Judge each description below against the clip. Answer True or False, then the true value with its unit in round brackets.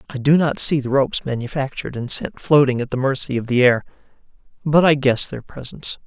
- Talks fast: True (210 wpm)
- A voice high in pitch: False (135 Hz)